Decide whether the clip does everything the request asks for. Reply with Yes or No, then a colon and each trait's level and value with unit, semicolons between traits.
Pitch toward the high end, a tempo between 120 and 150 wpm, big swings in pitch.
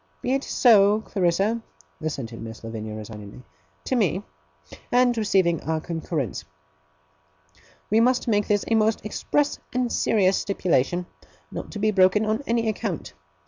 Yes: high, 200 Hz; average, 140 wpm; wide, 6.0 semitones